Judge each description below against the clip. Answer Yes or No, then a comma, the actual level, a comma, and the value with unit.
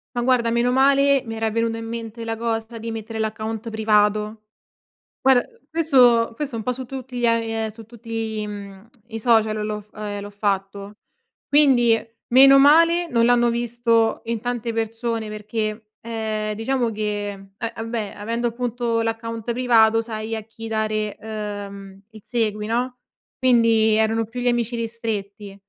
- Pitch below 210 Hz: No, high, 225 Hz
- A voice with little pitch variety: Yes, narrow, 1.8 semitones